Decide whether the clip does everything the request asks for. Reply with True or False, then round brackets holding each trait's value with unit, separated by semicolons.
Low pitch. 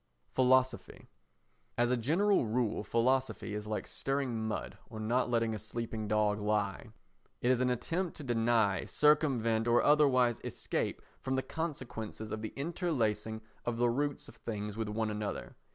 True (120 Hz)